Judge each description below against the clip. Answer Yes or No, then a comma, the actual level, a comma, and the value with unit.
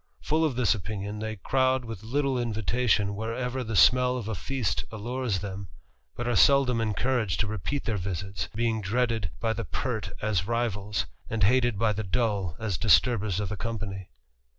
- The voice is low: Yes, low, 110 Hz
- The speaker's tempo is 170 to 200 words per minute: Yes, average, 175 wpm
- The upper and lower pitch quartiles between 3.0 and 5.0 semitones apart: Yes, average, 3.5 semitones